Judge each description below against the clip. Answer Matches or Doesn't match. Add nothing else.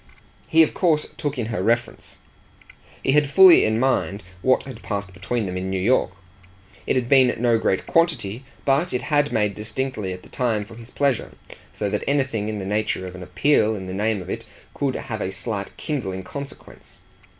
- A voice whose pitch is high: Doesn't match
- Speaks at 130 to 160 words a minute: Doesn't match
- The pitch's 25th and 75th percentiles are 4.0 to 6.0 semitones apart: Matches